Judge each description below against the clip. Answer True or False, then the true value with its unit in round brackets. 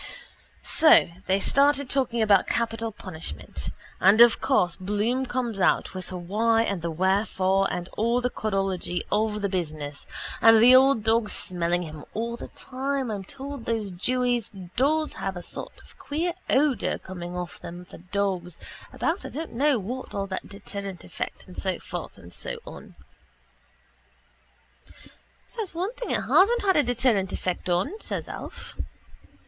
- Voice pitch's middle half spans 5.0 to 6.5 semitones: True (5.5 semitones)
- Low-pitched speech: False (215 Hz)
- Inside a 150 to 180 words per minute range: True (155 wpm)